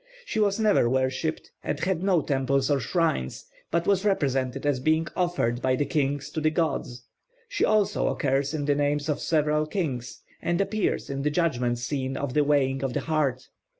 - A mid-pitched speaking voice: Yes, medium, 145 Hz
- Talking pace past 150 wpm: Yes, average, 185 wpm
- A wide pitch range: No, average, 3.8 semitones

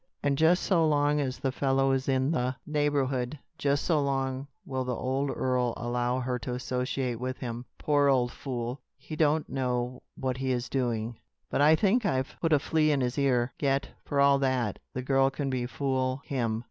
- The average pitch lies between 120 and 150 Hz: Yes, low, 135 Hz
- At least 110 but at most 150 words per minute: No, average, 190 wpm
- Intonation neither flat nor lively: No, narrow, 2.2 semitones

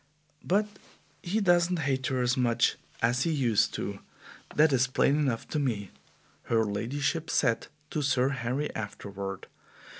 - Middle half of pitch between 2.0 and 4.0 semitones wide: No, average, 4.4 semitones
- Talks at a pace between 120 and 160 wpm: Yes, average, 145 wpm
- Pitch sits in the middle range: No, low, 130 Hz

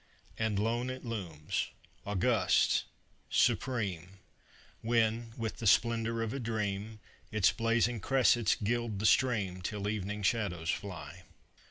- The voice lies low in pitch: Yes, low, 110 Hz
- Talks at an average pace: No, slow, 120 wpm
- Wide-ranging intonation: No, average, 2.9 semitones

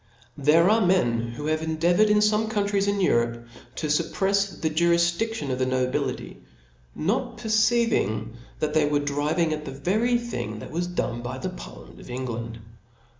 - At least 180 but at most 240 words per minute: No, average, 165 wpm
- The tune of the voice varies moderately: No, wide, 7.7 semitones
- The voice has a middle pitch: Yes, medium, 160 Hz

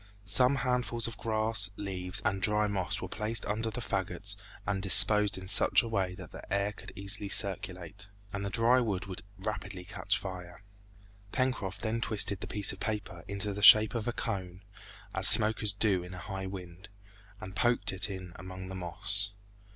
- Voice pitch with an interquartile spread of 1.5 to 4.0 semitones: Yes, narrow, 2.6 semitones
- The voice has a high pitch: No, low, 100 Hz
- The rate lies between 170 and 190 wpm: Yes, average, 180 wpm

